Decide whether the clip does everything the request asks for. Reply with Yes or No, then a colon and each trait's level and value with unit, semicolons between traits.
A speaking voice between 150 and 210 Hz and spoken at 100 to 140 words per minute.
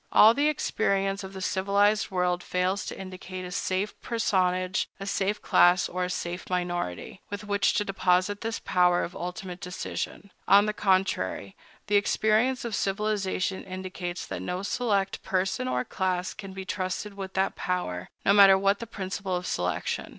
No: high, 190 Hz; average, 165 wpm